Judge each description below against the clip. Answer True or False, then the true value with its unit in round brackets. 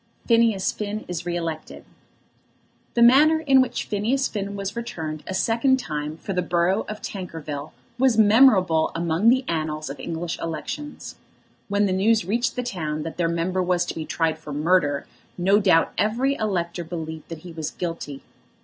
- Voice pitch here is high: False (180 Hz)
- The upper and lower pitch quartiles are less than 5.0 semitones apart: False (5.3 semitones)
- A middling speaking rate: True (170 wpm)